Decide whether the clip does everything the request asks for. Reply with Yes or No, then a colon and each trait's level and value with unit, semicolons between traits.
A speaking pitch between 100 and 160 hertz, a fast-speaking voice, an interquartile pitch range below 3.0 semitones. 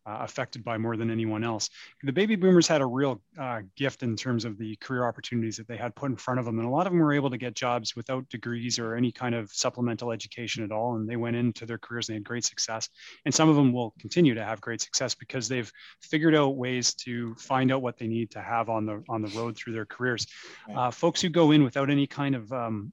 Yes: low, 120 Hz; fast, 265 wpm; narrow, 2.6 semitones